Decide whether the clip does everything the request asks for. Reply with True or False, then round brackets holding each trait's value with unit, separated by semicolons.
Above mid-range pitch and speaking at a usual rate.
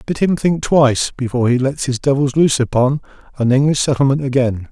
False (135 Hz; 190 wpm)